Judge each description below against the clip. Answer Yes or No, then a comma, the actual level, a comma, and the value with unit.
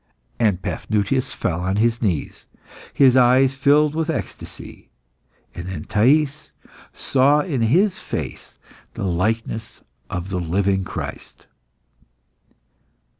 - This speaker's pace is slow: Yes, slow, 115 wpm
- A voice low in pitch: Yes, low, 115 Hz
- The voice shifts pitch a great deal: Yes, wide, 6.3 semitones